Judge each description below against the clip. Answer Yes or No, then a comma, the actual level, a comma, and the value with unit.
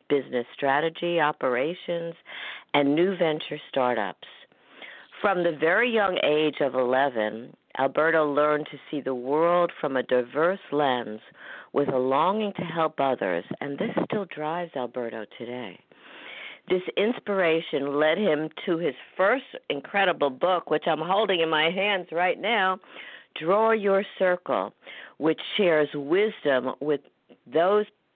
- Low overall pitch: No, medium, 155 Hz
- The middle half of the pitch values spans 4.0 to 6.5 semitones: Yes, average, 5.0 semitones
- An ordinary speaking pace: No, slow, 130 wpm